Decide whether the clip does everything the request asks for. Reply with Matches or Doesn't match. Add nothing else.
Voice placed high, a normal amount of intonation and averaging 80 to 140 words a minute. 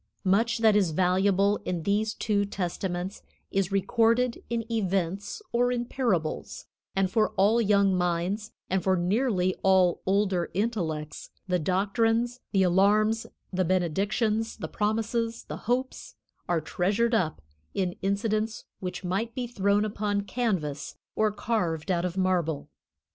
Matches